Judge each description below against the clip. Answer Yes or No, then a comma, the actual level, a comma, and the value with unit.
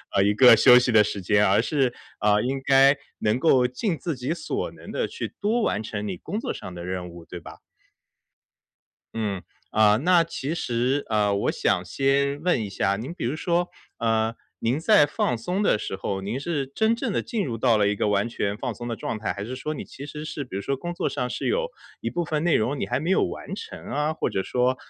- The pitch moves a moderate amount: No, wide, 6.6 semitones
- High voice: No, low, 125 Hz